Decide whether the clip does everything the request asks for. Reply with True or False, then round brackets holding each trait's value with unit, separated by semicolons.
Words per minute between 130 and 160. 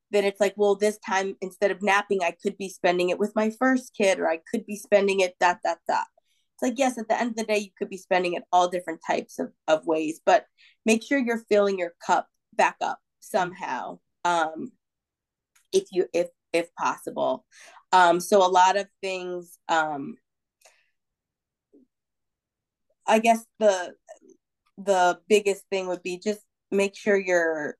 False (175 wpm)